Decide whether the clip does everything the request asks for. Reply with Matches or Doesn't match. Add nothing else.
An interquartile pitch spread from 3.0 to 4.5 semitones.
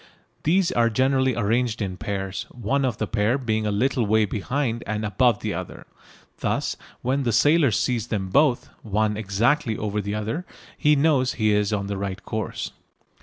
Matches